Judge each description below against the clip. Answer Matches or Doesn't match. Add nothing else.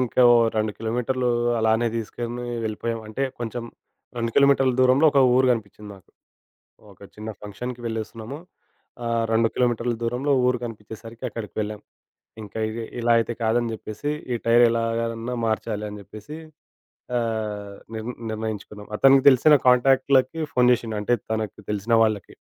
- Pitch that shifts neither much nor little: Doesn't match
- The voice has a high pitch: Doesn't match